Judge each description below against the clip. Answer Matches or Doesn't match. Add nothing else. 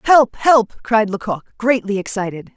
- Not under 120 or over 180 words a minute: Matches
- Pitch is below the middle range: Doesn't match